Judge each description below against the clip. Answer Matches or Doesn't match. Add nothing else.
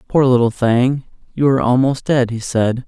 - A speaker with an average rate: Matches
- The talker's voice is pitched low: Matches